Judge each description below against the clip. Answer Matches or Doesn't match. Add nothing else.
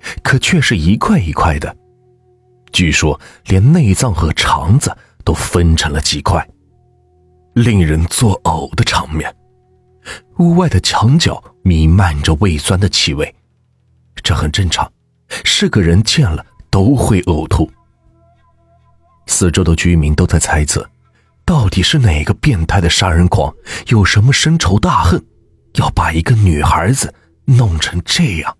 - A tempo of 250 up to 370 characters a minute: Doesn't match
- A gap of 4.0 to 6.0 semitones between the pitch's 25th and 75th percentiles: Matches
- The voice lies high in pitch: Doesn't match